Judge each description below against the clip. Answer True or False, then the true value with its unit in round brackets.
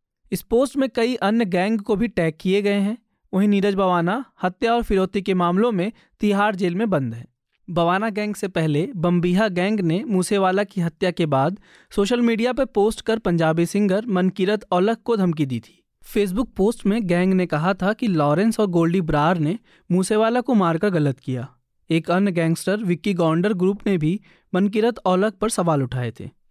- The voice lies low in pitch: False (190 Hz)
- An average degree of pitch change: True (3.6 semitones)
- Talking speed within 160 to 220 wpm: True (190 wpm)